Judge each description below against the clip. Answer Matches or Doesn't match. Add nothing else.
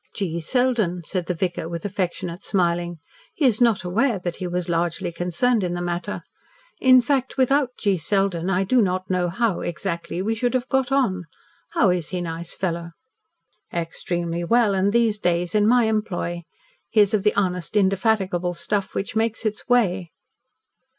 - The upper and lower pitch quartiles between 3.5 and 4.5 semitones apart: Matches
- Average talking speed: Matches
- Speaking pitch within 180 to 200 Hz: Matches